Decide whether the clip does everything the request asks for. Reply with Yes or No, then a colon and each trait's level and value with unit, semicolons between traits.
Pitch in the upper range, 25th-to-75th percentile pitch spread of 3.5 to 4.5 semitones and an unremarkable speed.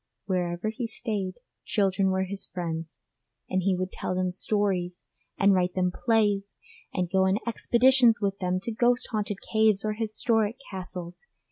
No: high, 195 Hz; average, 3.0 semitones; average, 155 wpm